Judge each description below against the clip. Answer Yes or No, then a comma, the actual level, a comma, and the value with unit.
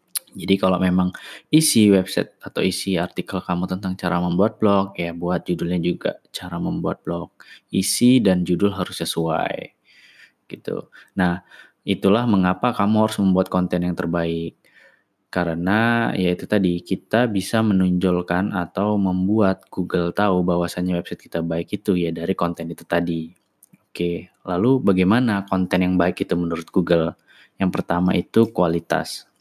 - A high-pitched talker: No, very low, 90 Hz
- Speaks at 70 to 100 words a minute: No, fast, 140 wpm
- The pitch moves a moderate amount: No, narrow, 2.1 semitones